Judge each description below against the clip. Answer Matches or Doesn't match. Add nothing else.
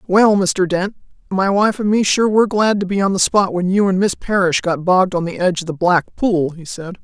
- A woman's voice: Matches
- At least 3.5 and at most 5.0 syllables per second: Doesn't match